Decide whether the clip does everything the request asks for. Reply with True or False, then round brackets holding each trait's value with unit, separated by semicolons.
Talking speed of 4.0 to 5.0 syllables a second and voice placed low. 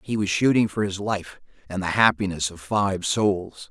True (4.5 syllables/s; 95 Hz)